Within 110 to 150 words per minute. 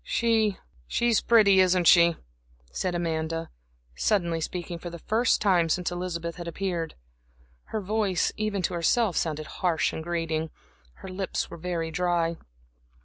Yes: average, 145 wpm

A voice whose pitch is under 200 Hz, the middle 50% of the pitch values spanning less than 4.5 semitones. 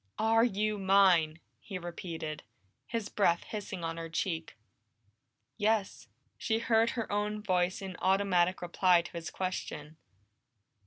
Yes: high, 190 Hz; average, 3.6 semitones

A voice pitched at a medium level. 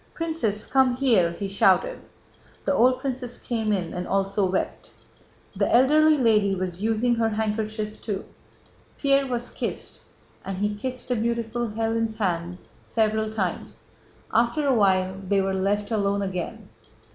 No: high, 220 Hz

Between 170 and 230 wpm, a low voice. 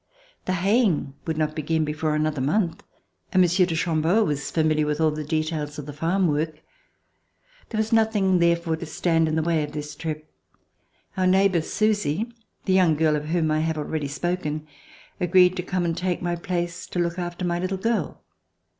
No: average, 190 wpm; medium, 165 Hz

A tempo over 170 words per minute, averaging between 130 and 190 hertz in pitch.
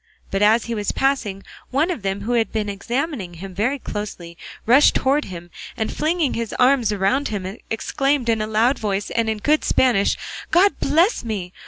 No: average, 180 wpm; high, 225 Hz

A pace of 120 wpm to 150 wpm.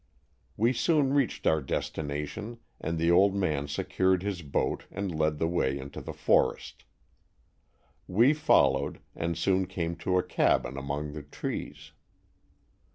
Yes: average, 145 wpm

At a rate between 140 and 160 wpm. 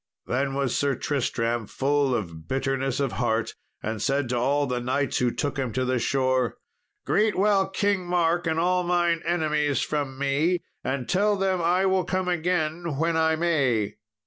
No: average, 175 wpm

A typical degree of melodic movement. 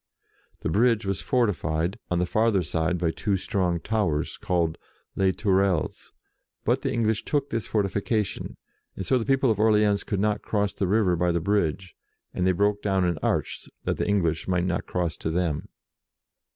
Yes: average, 3.4 semitones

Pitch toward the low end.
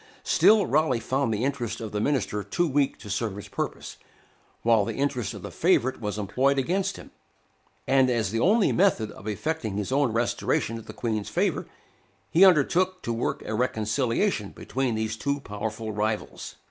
Yes: low, 120 Hz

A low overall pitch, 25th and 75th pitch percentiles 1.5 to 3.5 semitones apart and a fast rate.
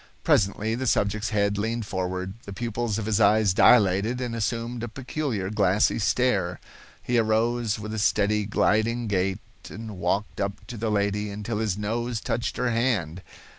No: low, 110 Hz; narrow, 2.5 semitones; average, 165 wpm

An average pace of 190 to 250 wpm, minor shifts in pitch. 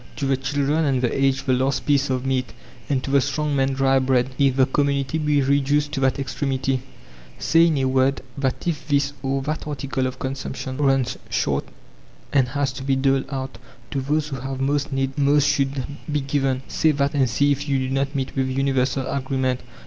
Yes: fast, 205 wpm; narrow, 1.2 semitones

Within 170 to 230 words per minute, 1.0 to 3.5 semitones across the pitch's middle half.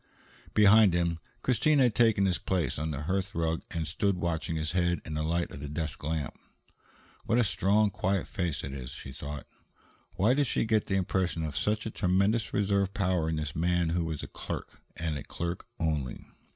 No: average, 200 wpm; average, 3.9 semitones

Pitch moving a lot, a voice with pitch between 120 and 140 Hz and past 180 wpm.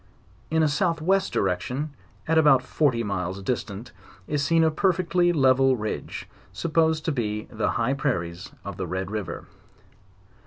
No: wide, 7.2 semitones; low, 135 Hz; average, 150 wpm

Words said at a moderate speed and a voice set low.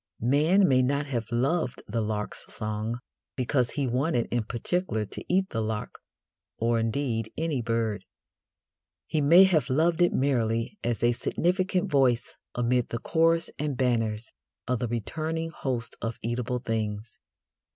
Yes: average, 145 wpm; low, 125 Hz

